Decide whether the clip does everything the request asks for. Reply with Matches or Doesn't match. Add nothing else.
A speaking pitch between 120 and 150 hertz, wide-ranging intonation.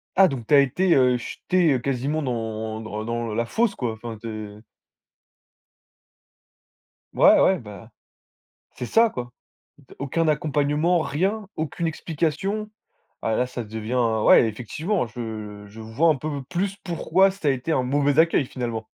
Matches